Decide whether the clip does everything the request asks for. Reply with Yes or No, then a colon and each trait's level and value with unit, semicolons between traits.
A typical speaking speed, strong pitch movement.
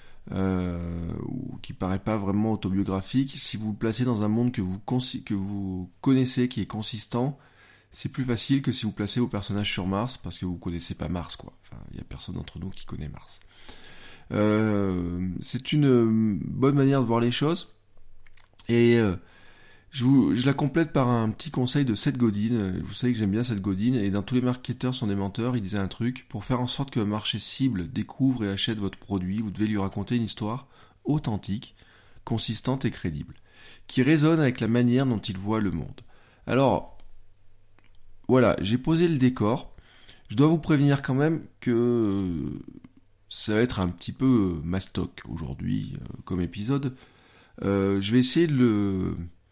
No: average, 185 wpm; average, 4.3 semitones